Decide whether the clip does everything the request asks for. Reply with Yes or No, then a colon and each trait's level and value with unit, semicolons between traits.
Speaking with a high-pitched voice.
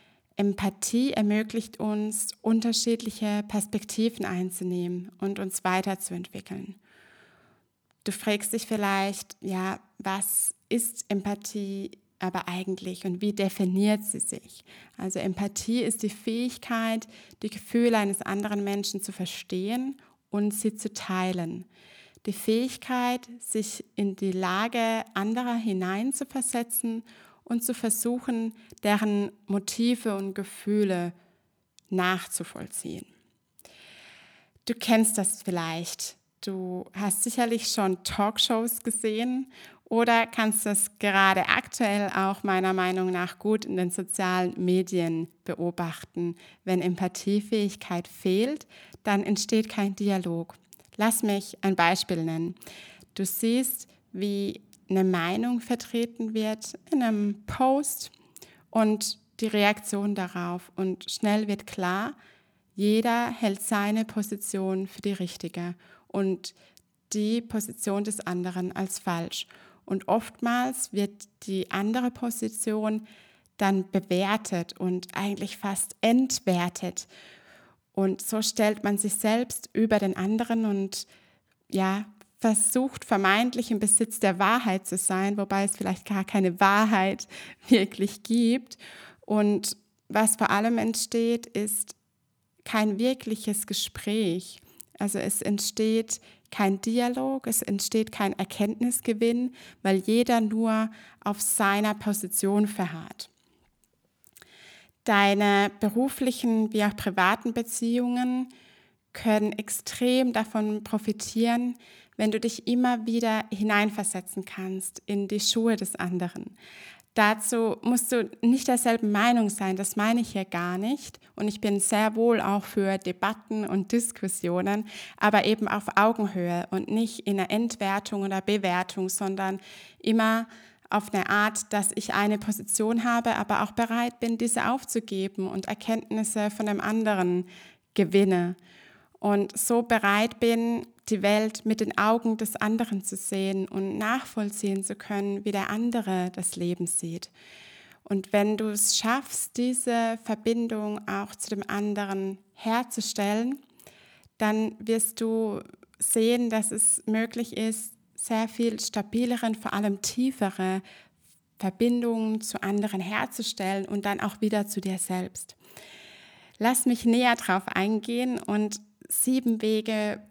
Yes: high, 210 Hz